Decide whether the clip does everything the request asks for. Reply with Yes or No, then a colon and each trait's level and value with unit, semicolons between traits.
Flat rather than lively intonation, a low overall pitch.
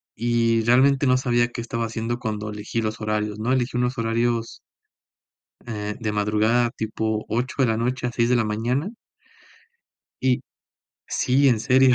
Yes: narrow, 2.1 semitones; low, 115 Hz